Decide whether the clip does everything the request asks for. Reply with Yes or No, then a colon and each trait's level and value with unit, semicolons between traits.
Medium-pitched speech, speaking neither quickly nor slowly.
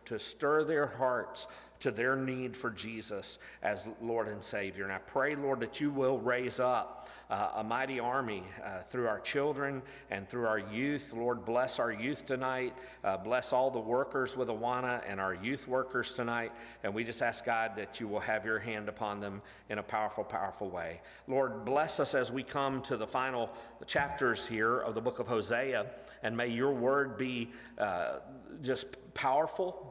No: low, 125 Hz; average, 185 wpm